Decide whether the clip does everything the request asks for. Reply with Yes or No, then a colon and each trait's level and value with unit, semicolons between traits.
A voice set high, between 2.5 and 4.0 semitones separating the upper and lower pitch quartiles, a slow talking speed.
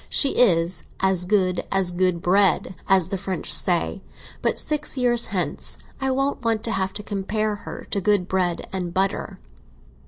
No: high, 195 Hz; average, 2.9 semitones; average, 165 wpm